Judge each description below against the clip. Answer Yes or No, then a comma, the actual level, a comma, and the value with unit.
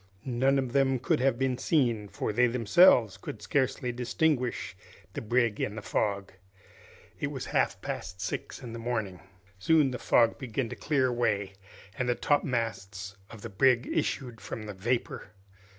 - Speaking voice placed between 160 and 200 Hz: No, low, 120 Hz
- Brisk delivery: No, average, 165 wpm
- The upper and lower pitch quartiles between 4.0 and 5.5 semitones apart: No, average, 3.6 semitones